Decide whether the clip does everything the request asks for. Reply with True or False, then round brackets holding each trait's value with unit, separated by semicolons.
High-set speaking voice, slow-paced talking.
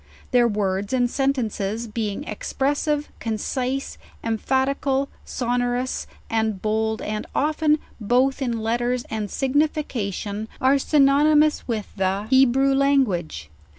True (245 Hz; 110 wpm)